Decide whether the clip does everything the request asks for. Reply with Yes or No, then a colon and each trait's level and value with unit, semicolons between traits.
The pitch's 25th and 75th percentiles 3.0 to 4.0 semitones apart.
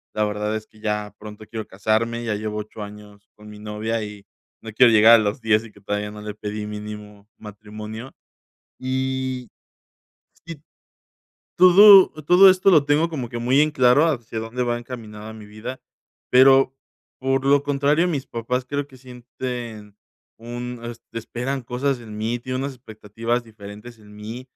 Yes: average, 3.5 semitones